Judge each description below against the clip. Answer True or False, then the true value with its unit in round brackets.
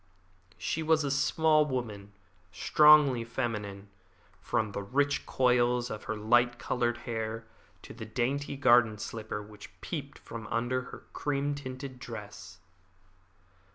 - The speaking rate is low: True (125 wpm)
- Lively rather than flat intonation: False (3.8 semitones)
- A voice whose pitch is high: False (120 Hz)